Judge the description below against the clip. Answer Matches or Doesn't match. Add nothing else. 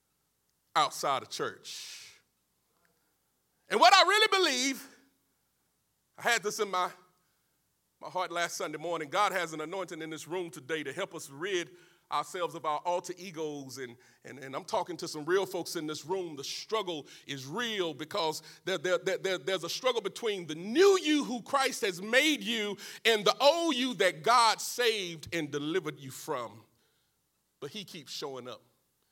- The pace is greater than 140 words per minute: Matches